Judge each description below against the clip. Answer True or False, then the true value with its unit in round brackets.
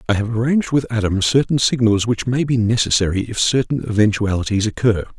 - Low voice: True (115 Hz)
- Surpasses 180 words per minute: False (175 wpm)